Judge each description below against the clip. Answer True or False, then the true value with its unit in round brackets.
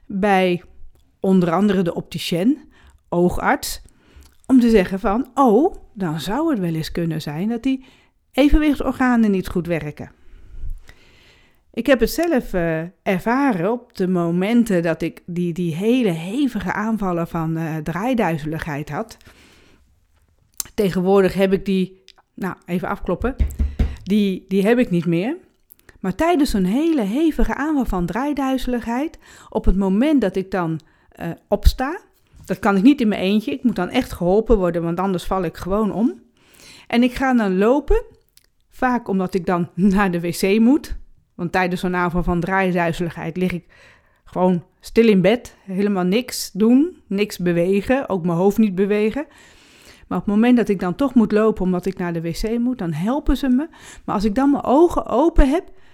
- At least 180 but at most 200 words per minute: False (165 wpm)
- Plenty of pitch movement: True (5.8 semitones)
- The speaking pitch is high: True (200 Hz)